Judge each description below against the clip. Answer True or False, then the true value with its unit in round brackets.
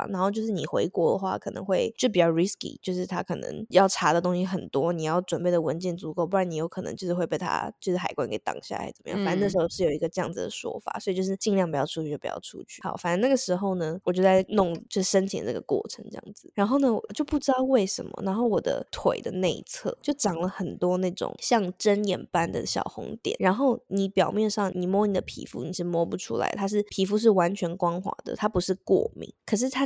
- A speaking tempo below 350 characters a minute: False (370 characters per minute)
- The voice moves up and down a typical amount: True (3.1 semitones)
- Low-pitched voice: False (190 Hz)